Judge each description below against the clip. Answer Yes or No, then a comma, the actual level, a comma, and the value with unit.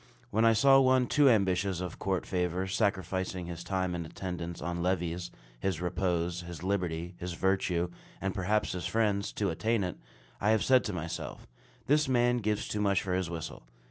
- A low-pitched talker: Yes, very low, 95 Hz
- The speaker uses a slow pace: No, average, 180 wpm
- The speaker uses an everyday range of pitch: Yes, average, 3.3 semitones